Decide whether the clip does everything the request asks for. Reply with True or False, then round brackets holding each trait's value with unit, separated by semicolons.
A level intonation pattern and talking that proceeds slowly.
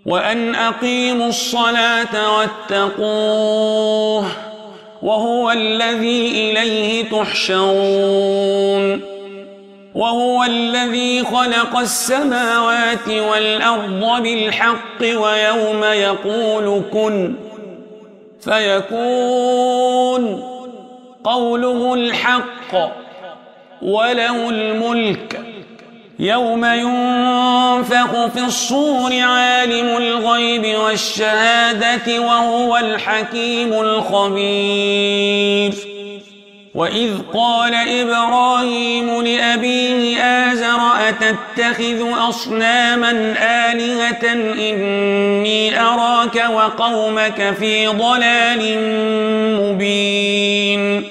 True (1.9 semitones; 55 wpm)